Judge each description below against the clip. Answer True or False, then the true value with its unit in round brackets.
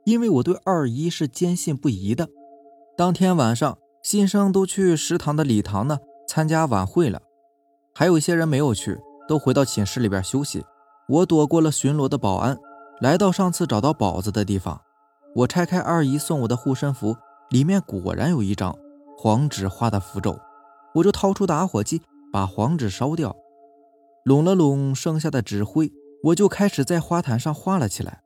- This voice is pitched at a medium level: True (145 Hz)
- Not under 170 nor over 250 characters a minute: False (265 characters per minute)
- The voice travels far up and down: True (6.9 semitones)